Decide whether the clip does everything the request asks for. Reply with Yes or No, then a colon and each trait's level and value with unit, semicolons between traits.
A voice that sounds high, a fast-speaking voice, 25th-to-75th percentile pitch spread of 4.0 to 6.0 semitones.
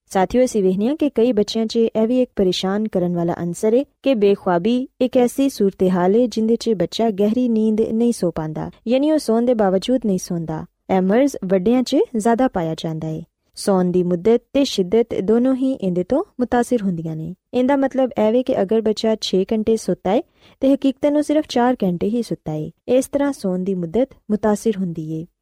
Yes: high, 225 Hz; fast, 190 wpm; average, 5.0 semitones